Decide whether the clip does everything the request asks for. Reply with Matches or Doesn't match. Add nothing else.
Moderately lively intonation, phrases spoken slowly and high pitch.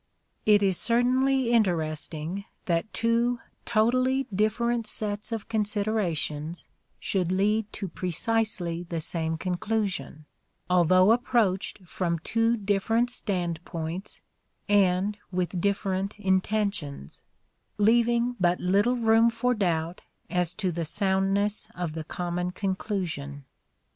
Matches